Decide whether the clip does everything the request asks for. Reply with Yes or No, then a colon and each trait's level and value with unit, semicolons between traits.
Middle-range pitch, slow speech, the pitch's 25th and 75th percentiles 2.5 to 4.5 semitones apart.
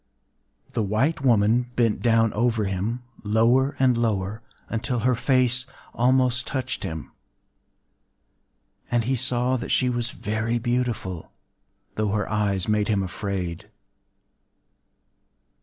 No: low, 115 Hz; slow, 110 wpm; average, 3.0 semitones